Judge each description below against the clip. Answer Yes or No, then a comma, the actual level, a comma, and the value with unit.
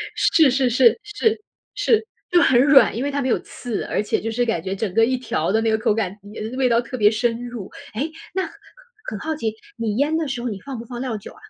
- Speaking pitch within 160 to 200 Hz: No, high, 240 Hz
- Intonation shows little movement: No, average, 3.7 semitones